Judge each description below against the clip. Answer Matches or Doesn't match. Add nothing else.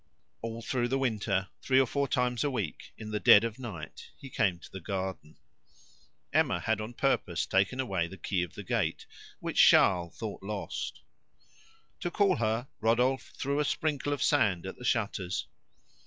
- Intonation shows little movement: Doesn't match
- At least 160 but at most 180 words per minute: Matches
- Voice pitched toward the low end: Matches